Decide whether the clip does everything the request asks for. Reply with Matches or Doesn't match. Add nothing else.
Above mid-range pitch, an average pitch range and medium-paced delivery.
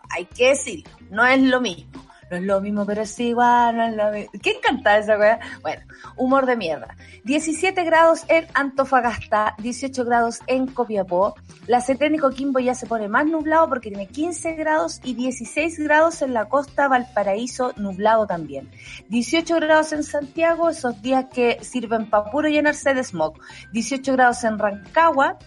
Doesn't match